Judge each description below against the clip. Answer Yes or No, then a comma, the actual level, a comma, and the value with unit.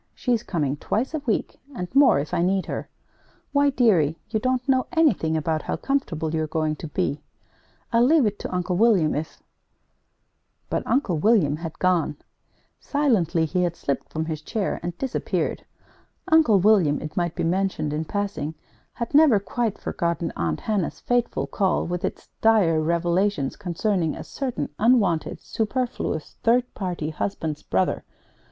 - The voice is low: No, medium, 180 Hz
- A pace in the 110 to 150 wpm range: No, average, 160 wpm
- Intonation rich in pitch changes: Yes, wide, 6.4 semitones